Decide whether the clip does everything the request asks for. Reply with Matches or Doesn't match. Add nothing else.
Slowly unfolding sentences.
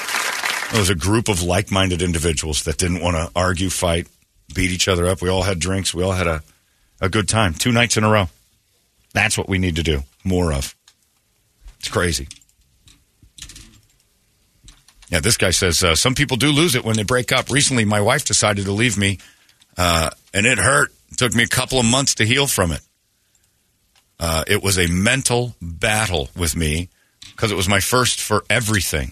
Doesn't match